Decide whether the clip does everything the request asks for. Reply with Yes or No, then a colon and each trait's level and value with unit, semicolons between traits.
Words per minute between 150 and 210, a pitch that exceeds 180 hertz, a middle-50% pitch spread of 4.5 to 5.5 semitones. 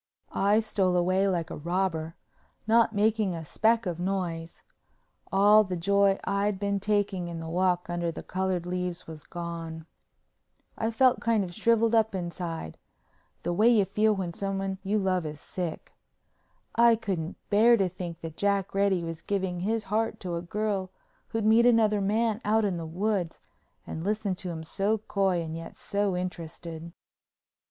No: average, 165 wpm; high, 190 Hz; average, 3.4 semitones